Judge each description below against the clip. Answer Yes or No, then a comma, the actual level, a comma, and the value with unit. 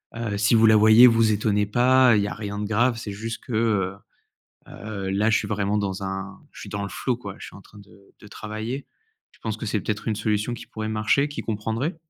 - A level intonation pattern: Yes, narrow, 1.9 semitones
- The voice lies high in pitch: No, low, 110 Hz